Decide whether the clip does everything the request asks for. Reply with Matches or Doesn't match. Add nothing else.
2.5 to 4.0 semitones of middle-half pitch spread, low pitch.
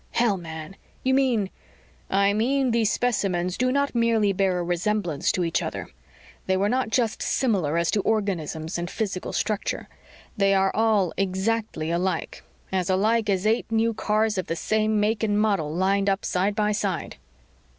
Doesn't match